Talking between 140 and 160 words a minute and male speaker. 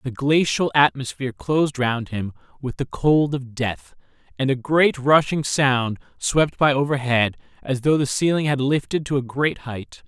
No: average, 175 wpm; male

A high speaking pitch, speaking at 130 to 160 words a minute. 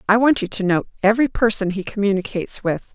No: high, 205 Hz; fast, 205 wpm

